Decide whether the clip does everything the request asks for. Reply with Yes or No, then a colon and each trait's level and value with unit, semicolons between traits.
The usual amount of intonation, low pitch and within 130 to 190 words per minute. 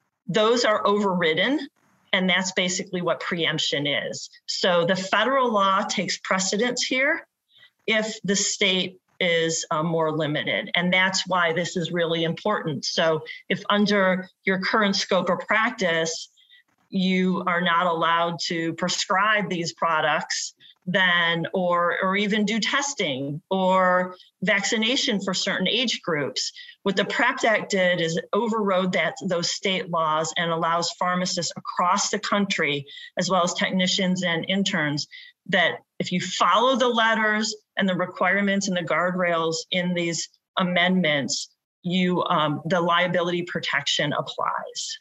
No: average, 3.2 semitones; medium, 185 Hz; slow, 135 wpm